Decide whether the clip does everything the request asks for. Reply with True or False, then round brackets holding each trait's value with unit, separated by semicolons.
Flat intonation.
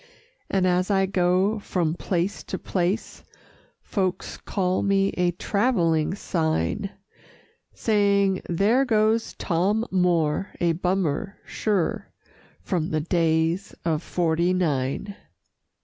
False (3.0 semitones)